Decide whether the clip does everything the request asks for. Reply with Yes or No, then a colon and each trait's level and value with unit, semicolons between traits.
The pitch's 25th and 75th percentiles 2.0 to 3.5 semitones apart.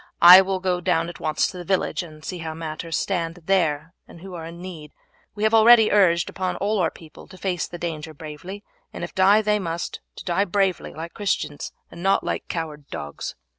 Yes: average, 2.9 semitones